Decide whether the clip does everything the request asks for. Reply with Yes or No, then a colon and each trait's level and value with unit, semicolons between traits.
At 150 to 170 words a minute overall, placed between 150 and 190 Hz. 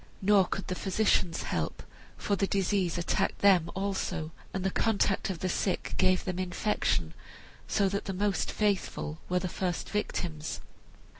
Yes: average, 155 wpm; medium, 185 Hz